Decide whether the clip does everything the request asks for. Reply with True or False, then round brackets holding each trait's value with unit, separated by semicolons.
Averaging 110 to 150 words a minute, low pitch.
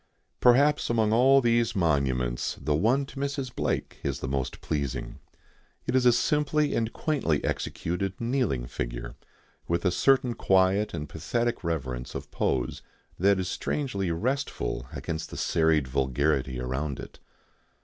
True (140 wpm; 90 Hz)